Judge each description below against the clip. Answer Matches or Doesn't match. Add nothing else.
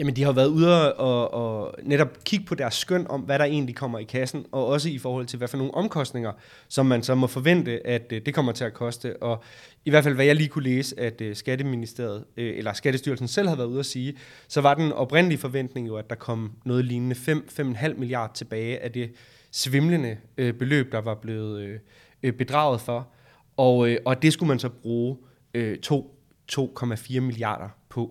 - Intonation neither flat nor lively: Matches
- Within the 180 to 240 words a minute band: Matches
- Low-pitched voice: Matches